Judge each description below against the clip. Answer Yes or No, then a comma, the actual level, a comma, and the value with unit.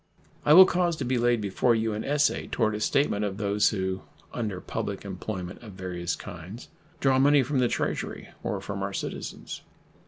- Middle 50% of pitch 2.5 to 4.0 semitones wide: No, average, 5.2 semitones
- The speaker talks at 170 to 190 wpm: Yes, average, 185 wpm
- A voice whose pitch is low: Yes, low, 110 Hz